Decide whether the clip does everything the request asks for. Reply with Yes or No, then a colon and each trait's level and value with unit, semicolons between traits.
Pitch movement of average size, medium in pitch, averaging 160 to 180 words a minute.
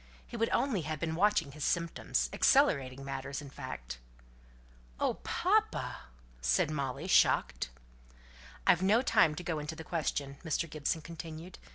No: average, 3.7 semitones; medium, 155 Hz; average, 145 wpm